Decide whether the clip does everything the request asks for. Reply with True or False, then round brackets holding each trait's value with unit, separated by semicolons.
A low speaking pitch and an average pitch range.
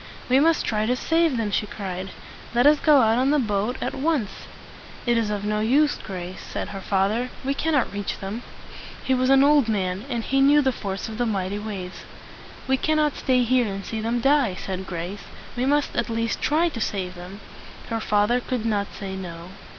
False (225 Hz; 5.0 semitones)